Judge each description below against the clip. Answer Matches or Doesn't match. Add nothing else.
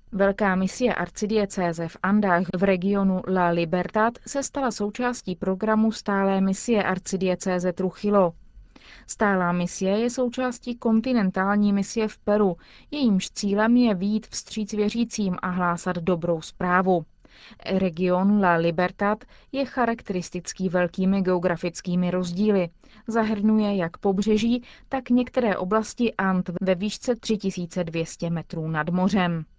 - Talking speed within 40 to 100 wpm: Doesn't match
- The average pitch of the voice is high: Matches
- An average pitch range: Matches